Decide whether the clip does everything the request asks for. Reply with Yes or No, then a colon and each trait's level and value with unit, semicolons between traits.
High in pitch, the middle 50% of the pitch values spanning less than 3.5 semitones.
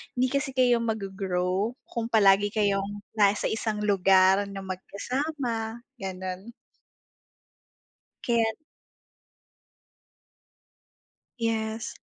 Yes: high, 210 Hz; average, 3.0 semitones